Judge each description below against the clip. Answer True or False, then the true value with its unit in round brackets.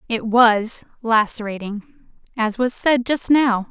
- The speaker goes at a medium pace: False (130 wpm)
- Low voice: False (230 Hz)